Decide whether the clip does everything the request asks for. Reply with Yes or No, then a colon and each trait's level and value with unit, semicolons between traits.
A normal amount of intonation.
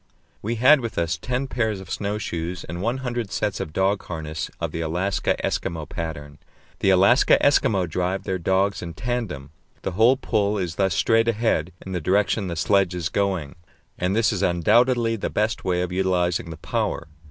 Yes: average, 4.2 semitones